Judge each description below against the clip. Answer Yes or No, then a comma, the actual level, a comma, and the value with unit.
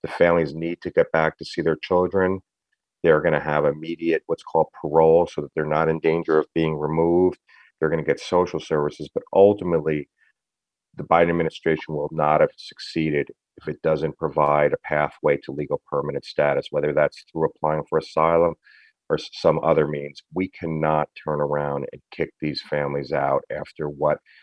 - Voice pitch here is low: Yes, very low, 80 Hz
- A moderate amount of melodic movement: No, narrow, 2.0 semitones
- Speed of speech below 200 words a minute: Yes, average, 180 wpm